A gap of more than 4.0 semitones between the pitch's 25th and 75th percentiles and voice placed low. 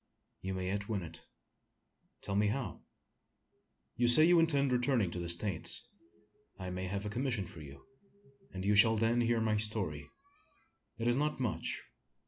Yes: average, 4.5 semitones; low, 105 Hz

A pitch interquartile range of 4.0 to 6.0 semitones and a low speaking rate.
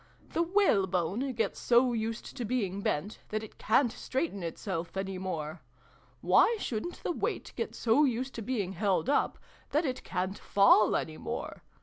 No: average, 5.1 semitones; average, 160 wpm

